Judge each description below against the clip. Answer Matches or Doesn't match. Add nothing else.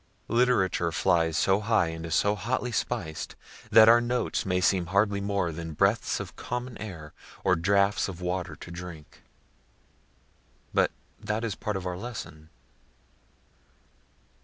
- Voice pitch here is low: Matches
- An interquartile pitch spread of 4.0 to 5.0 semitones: Matches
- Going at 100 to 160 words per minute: Matches